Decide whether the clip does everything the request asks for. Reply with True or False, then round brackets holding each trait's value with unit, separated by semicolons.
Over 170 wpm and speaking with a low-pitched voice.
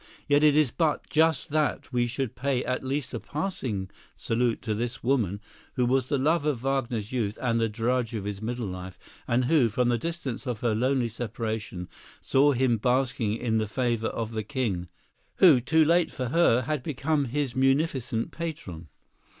True (180 wpm; 125 Hz)